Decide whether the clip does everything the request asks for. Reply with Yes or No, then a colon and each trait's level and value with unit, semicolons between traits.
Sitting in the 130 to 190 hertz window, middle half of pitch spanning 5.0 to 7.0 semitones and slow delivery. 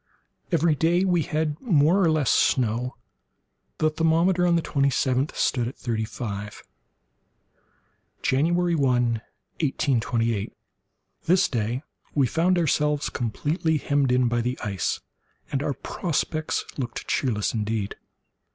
Yes: medium, 140 Hz; average, 5.3 semitones; slow, 120 wpm